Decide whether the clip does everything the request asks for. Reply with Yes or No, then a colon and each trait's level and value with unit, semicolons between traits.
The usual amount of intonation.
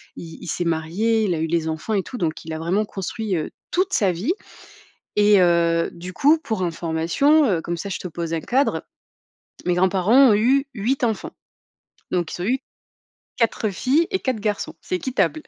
No: wide, 5.9 semitones